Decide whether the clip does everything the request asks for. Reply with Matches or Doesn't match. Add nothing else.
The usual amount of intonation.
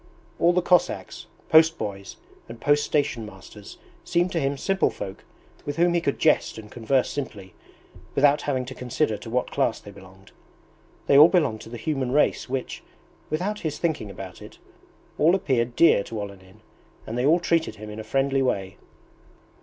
Doesn't match